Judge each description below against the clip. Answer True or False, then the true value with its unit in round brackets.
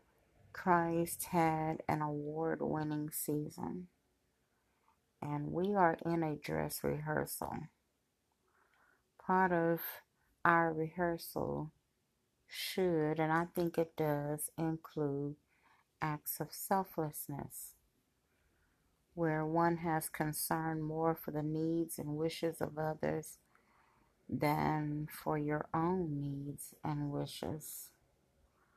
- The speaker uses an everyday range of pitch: False (2.1 semitones)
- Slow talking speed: True (95 wpm)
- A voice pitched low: False (155 Hz)